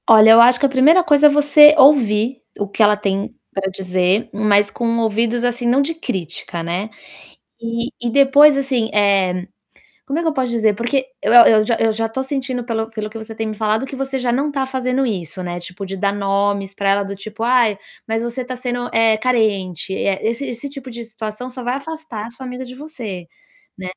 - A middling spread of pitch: Yes, average, 4.2 semitones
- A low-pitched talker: No, high, 230 Hz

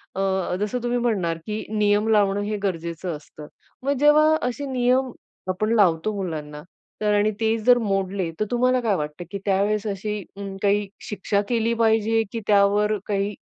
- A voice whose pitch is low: No, high, 210 Hz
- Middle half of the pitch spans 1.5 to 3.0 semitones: Yes, narrow, 2.6 semitones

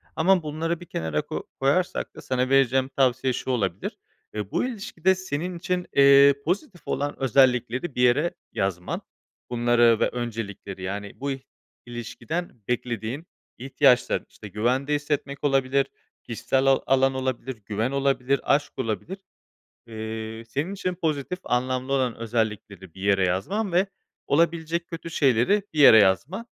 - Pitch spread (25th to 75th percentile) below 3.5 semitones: No, average, 5.3 semitones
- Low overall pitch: Yes, low, 130 Hz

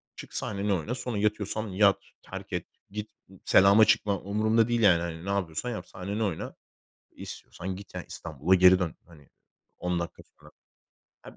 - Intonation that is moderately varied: Yes, average, 3.1 semitones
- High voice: No, low, 100 Hz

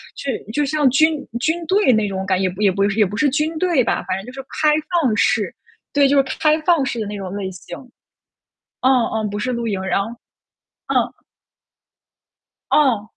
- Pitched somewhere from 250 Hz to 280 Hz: Yes, very high, 255 Hz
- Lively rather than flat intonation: Yes, wide, 6.9 semitones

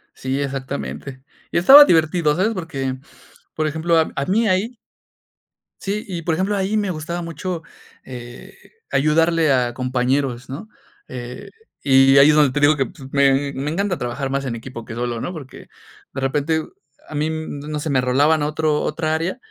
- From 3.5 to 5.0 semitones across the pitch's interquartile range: Yes, average, 3.8 semitones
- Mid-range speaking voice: Yes, medium, 150 Hz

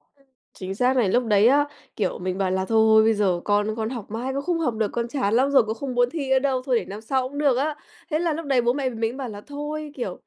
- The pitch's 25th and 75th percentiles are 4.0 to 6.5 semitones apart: Yes, average, 4.3 semitones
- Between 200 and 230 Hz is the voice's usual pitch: No, high, 245 Hz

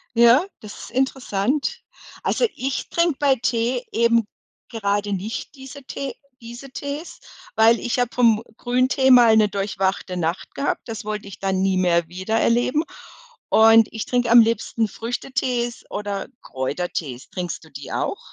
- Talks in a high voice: Yes, high, 230 Hz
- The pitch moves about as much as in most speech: Yes, average, 4.2 semitones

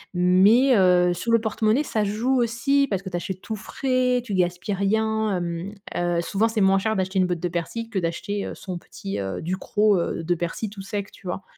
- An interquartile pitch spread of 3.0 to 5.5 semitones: Yes, average, 3.7 semitones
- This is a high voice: Yes, high, 195 Hz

